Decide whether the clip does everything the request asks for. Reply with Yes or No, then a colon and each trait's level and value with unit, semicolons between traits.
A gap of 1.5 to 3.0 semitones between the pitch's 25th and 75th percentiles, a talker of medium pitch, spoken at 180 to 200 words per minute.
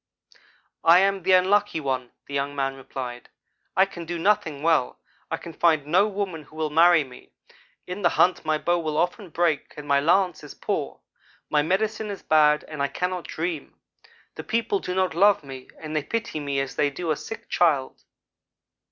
No: average, 4.1 semitones; medium, 165 Hz; average, 195 wpm